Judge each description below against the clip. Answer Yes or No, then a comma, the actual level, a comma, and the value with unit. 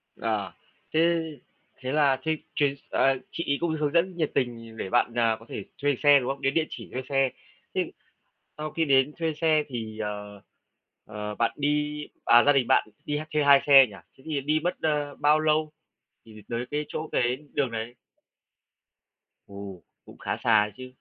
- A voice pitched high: No, medium, 140 Hz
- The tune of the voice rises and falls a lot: No, average, 4.6 semitones